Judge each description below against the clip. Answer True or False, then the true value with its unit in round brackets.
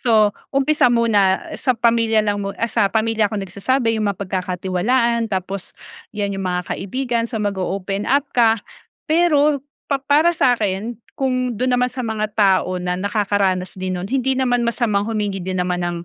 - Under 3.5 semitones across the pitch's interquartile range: False (4.1 semitones)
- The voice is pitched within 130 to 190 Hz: False (215 Hz)